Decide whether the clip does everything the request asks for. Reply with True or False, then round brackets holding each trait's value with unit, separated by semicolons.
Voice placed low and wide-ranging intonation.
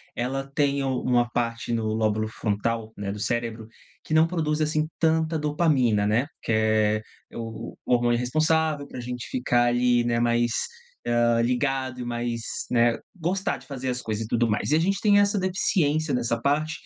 False (125 Hz; 4.7 semitones)